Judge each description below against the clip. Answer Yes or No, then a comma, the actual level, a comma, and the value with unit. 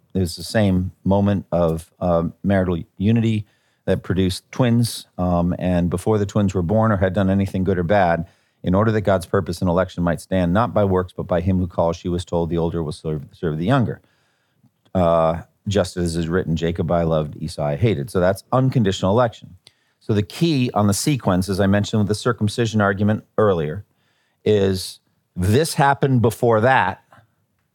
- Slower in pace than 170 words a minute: No, average, 185 wpm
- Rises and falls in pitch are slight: No, average, 3.8 semitones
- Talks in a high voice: No, very low, 95 Hz